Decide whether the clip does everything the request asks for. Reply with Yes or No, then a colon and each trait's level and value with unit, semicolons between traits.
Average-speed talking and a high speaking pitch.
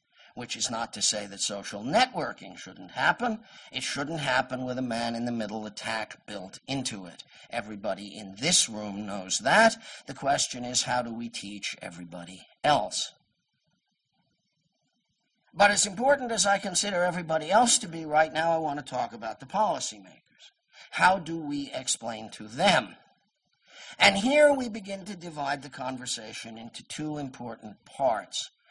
No: average, 155 wpm; medium, 140 Hz